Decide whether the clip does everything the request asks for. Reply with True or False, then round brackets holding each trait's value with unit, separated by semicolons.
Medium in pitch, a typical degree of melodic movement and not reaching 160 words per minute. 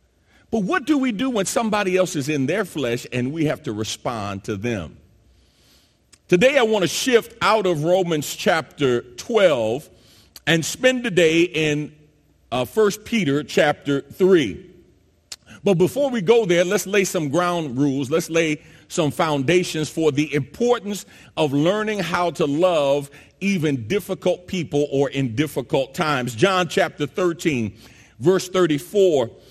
True (165 Hz; 4.7 semitones; 150 wpm)